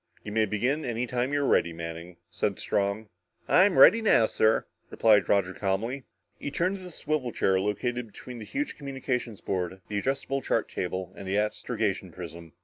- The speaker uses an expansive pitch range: Yes, wide, 5.8 semitones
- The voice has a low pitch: Yes, low, 110 Hz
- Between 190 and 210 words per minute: No, average, 180 wpm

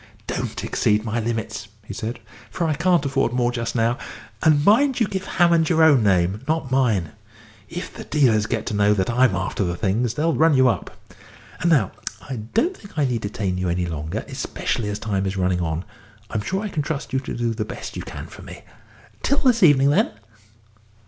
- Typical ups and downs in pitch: No, wide, 7.2 semitones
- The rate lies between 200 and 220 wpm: Yes, fast, 205 wpm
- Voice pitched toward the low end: Yes, low, 120 Hz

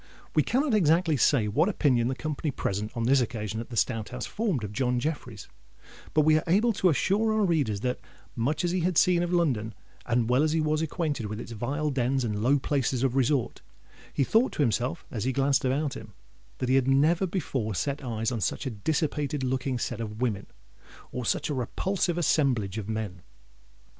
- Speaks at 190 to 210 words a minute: Yes, fast, 205 wpm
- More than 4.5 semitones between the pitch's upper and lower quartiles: Yes, average, 5.1 semitones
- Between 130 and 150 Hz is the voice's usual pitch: Yes, low, 135 Hz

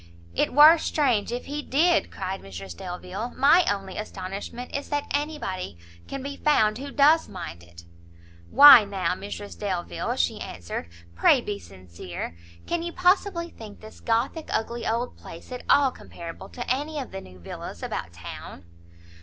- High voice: Yes, high, 220 Hz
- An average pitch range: No, wide, 7.9 semitones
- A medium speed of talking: Yes, average, 160 wpm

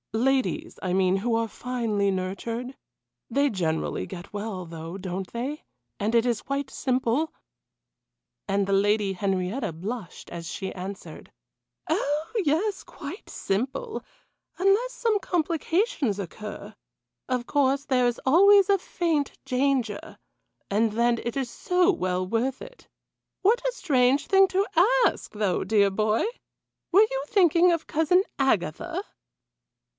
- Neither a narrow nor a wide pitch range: No, wide, 7.9 semitones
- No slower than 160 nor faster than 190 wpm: No, slow, 135 wpm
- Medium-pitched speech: No, high, 245 Hz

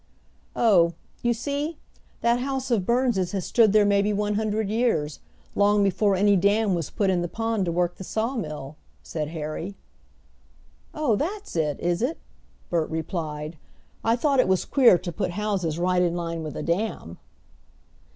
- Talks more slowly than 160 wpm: No, average, 165 wpm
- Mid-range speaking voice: No, high, 200 Hz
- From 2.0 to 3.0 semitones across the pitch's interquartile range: No, average, 4.9 semitones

